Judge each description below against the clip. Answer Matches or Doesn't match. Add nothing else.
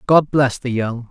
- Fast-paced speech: Matches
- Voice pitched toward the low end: Matches